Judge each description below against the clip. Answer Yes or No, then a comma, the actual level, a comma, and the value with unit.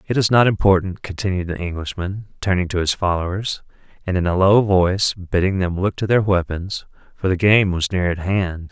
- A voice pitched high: No, very low, 95 Hz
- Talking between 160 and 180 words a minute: No, average, 200 wpm